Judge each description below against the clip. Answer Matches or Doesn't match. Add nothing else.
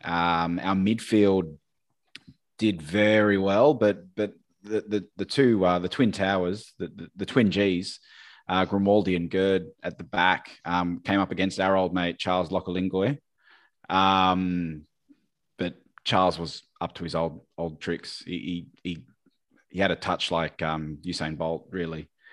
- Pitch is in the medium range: Doesn't match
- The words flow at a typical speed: Matches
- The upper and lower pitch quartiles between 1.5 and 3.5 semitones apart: Matches